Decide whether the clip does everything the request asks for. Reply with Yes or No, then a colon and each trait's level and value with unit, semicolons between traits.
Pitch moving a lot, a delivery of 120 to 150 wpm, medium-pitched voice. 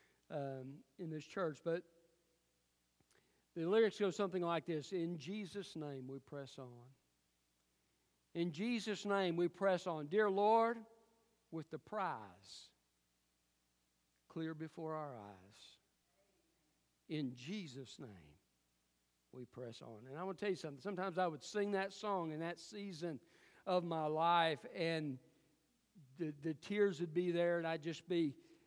Yes: wide, 6.3 semitones; average, 140 wpm; medium, 160 Hz